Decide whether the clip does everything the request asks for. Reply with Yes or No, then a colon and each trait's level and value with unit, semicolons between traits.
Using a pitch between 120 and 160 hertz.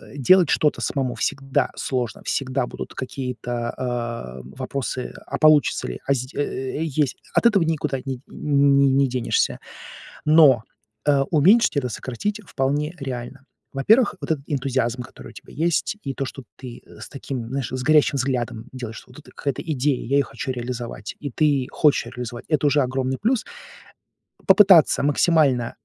Yes: low, 135 Hz